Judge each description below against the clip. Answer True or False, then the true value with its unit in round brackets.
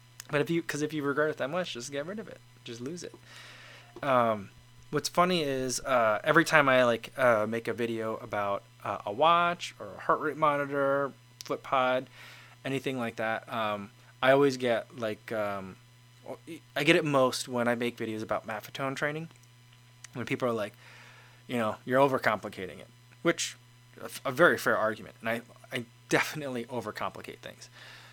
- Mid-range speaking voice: False (125 Hz)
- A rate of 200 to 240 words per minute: False (175 wpm)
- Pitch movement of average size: True (3.2 semitones)